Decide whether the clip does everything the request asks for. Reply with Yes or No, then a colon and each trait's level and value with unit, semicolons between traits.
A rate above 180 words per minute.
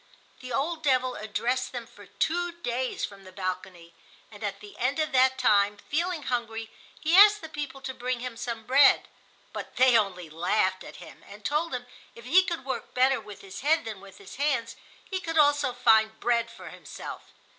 Yes: average, 195 wpm